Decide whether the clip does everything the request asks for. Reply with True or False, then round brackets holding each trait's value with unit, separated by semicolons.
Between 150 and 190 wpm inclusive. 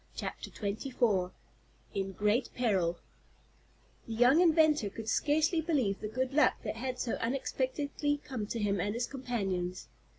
False (140 wpm)